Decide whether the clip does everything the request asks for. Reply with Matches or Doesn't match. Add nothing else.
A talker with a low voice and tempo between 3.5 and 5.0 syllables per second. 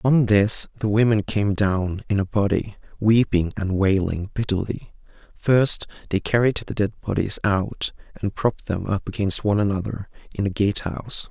Matches